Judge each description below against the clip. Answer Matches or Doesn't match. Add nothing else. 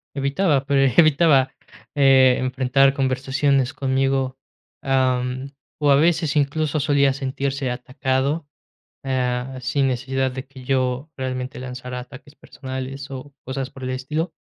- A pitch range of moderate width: Doesn't match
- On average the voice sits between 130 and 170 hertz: Matches